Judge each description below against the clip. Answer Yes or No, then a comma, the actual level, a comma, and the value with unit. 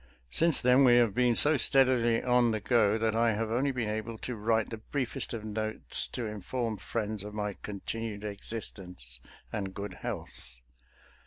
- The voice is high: No, low, 110 Hz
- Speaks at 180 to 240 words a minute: No, average, 170 wpm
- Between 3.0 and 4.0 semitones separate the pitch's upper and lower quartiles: No, narrow, 2.5 semitones